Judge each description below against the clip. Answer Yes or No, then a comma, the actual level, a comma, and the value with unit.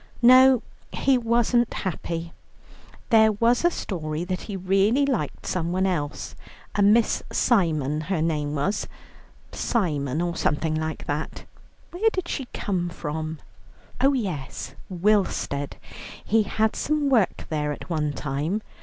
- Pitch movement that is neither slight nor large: No, wide, 6.8 semitones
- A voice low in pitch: No, medium, 185 Hz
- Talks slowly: Yes, slow, 130 wpm